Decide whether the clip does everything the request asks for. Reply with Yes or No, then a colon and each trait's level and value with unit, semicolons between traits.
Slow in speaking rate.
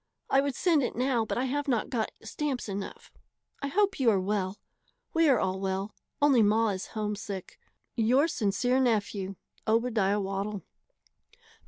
No: average, 155 wpm